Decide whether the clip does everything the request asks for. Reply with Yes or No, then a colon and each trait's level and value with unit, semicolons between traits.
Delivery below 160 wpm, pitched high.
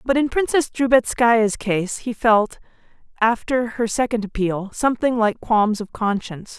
Yes: average, 145 wpm; high, 230 Hz